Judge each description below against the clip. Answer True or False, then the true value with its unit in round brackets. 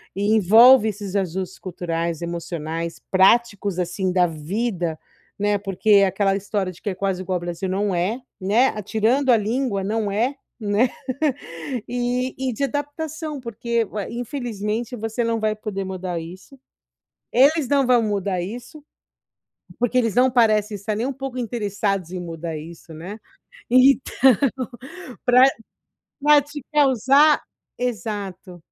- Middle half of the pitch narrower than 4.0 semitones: False (4.7 semitones)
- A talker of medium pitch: False (210 Hz)